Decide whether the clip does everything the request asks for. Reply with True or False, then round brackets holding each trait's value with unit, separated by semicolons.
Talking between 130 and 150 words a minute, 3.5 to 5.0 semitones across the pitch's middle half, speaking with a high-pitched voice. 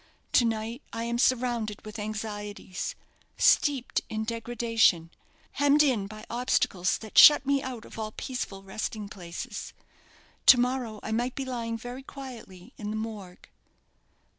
False (140 wpm; 3.0 semitones; 225 Hz)